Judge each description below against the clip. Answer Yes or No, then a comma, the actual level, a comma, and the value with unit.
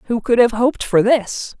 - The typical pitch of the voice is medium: No, high, 230 Hz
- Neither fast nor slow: No, fast, 225 wpm